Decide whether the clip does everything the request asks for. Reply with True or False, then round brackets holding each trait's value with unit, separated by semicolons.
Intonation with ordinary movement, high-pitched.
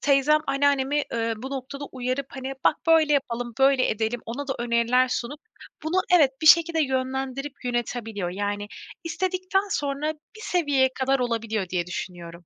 True (3.6 semitones; 265 Hz)